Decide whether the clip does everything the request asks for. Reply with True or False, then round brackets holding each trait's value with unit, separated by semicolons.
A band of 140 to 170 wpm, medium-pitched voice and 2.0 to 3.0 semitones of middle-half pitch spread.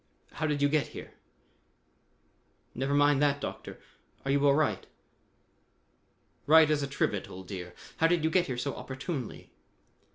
True (155 wpm; 145 Hz; 2.4 semitones)